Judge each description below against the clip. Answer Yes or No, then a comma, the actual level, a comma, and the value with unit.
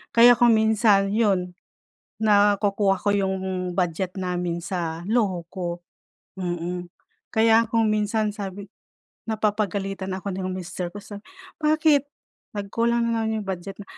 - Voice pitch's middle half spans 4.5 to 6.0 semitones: No, average, 3.0 semitones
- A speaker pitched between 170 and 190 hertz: No, high, 200 Hz